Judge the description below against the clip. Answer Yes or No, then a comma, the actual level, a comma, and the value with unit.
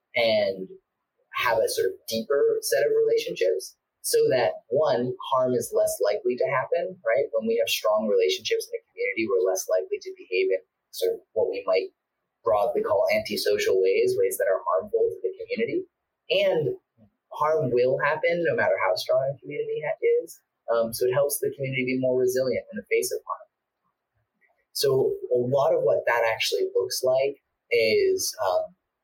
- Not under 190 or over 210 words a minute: No, average, 175 wpm